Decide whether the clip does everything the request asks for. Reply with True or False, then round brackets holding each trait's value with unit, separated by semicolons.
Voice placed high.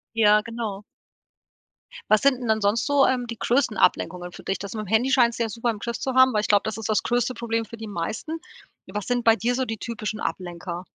True (225 Hz)